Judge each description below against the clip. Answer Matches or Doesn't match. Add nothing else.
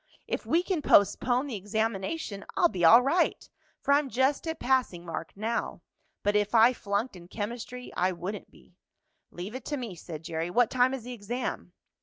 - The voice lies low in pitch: Doesn't match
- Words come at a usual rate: Matches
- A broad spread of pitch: Doesn't match